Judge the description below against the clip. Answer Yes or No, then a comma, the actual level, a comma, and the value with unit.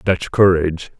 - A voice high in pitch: No, very low, 90 Hz